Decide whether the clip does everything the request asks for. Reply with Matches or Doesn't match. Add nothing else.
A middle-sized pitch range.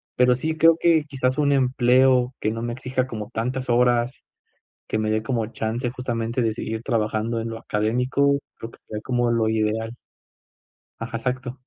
Doesn't match